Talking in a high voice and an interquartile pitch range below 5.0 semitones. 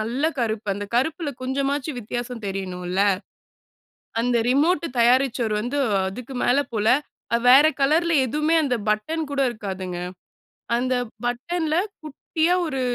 No: very high, 255 Hz; wide, 5.4 semitones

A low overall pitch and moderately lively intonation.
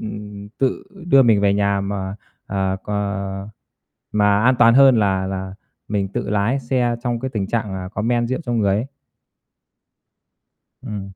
Yes: low, 105 Hz; average, 3.3 semitones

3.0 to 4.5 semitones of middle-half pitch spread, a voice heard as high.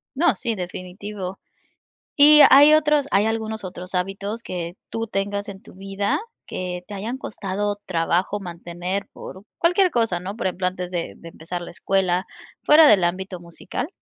Yes: average, 3.5 semitones; high, 195 Hz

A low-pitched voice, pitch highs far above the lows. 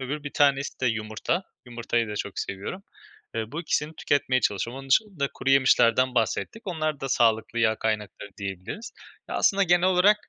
Yes: low, 130 Hz; wide, 5.7 semitones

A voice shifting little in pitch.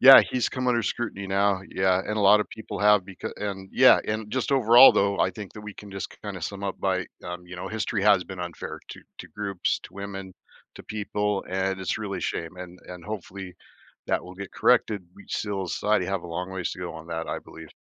Yes: narrow, 2.2 semitones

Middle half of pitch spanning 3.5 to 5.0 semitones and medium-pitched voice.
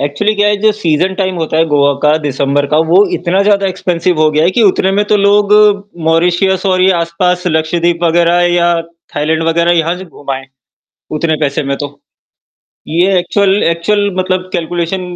No: average, 3.1 semitones; medium, 175 Hz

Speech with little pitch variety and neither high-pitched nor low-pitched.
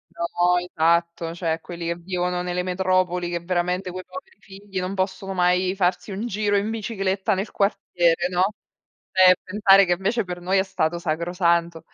Yes: narrow, 1.8 semitones; medium, 180 Hz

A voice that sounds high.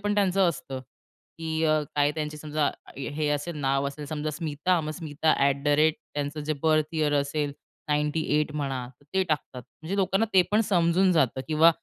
No: medium, 155 Hz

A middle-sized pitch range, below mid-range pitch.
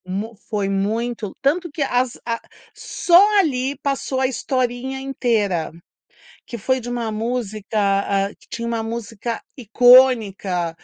No: average, 3.9 semitones; high, 235 Hz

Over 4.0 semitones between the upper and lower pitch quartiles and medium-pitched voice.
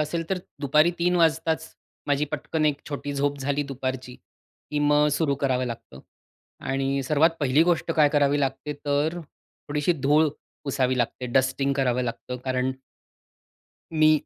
No: narrow, 2.6 semitones; medium, 145 Hz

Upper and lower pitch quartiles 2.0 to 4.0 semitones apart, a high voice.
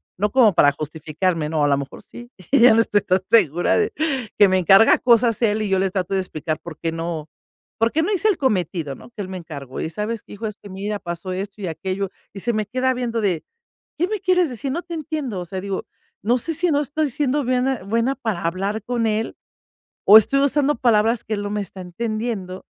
No: average, 5.2 semitones; high, 210 Hz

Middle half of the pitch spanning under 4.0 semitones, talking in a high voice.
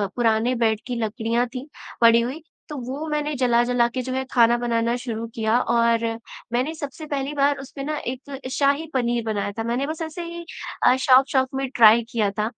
Yes: average, 3.0 semitones; very high, 250 Hz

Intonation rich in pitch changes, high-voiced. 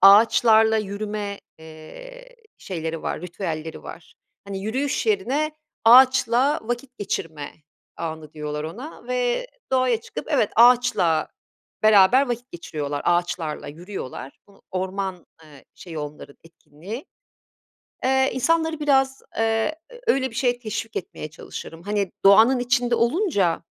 Yes: wide, 7.0 semitones; high, 215 Hz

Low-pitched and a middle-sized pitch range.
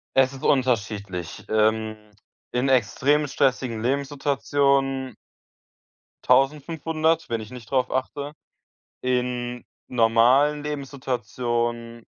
Yes: low, 130 Hz; average, 3.0 semitones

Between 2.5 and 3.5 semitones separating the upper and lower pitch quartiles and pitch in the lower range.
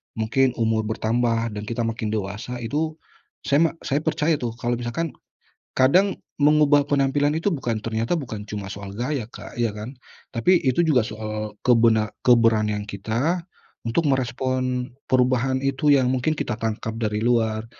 No: average, 4.0 semitones; low, 120 Hz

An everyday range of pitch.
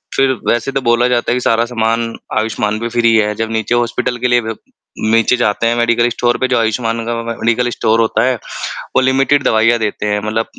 No: narrow, 1.4 semitones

